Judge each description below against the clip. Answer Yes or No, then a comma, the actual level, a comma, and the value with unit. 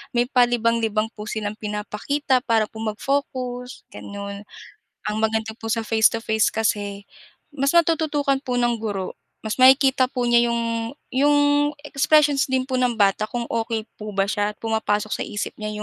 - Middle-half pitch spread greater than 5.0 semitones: No, average, 3.3 semitones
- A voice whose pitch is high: Yes, high, 230 Hz